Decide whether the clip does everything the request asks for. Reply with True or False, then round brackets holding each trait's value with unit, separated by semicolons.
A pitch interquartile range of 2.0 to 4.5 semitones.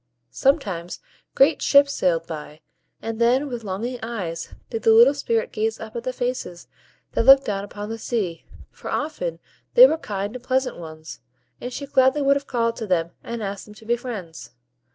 False (5.1 semitones)